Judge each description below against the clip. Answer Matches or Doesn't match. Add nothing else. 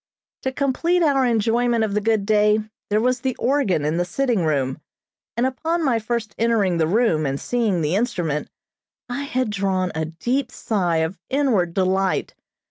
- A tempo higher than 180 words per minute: Doesn't match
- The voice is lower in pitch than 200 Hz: Doesn't match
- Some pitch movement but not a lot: Doesn't match